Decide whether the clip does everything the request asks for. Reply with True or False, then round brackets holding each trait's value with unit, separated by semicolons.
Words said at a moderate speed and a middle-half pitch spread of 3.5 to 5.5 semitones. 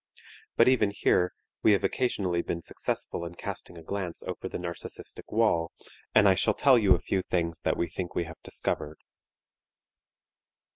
False (165 wpm; 3.0 semitones)